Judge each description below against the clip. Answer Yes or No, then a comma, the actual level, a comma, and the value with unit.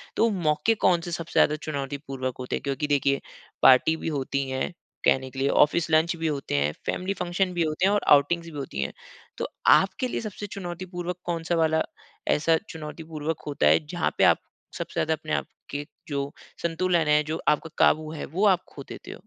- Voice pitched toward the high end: No, medium, 155 Hz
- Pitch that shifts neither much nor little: Yes, average, 3.7 semitones